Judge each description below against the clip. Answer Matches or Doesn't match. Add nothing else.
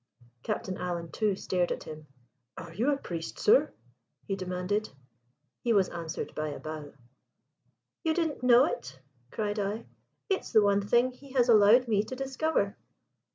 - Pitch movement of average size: Doesn't match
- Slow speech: Doesn't match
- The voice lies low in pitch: Doesn't match